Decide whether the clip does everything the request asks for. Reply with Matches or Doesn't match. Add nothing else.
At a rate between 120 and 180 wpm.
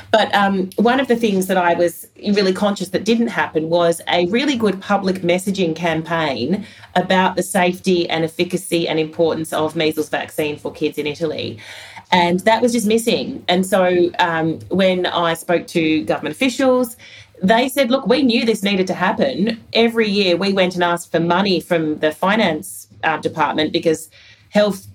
Matches